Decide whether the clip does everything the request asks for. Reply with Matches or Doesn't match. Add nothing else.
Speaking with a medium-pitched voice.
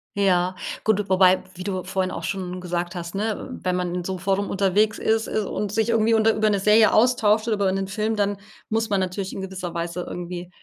Doesn't match